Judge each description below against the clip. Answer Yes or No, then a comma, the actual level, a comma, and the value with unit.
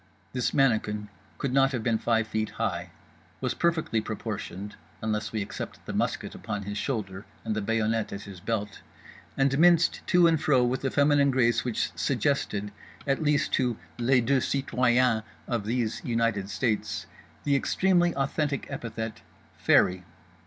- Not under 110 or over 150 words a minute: Yes, average, 145 wpm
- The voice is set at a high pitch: No, low, 115 Hz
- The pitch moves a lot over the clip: No, average, 4.2 semitones